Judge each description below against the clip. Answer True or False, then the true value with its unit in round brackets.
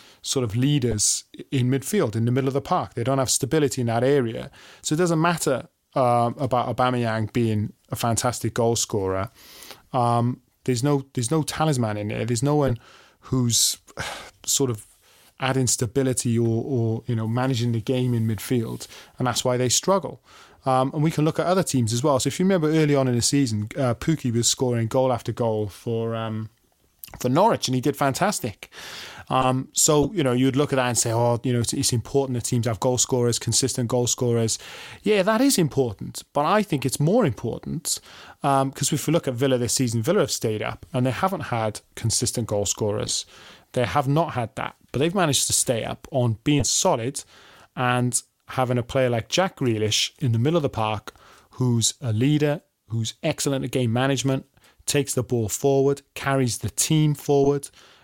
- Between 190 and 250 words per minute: True (205 wpm)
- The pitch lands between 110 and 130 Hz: True (125 Hz)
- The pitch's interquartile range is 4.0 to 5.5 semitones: False (3.1 semitones)